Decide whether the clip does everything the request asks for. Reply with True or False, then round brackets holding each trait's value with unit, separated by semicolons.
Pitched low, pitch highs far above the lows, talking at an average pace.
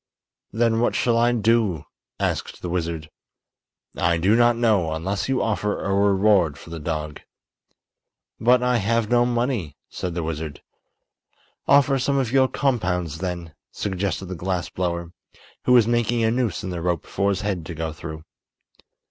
True (100 Hz; 5.7 semitones; 165 wpm)